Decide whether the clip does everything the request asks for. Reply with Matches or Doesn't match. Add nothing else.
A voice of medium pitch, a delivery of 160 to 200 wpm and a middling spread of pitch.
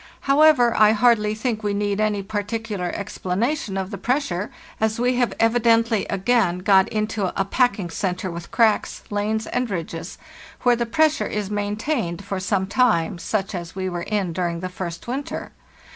Doesn't match